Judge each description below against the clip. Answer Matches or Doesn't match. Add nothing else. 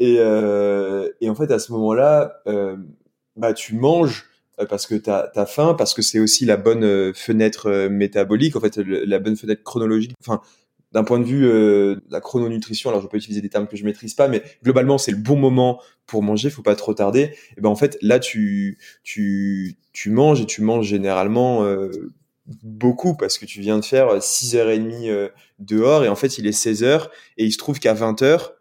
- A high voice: Doesn't match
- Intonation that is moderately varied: Matches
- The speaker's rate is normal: Matches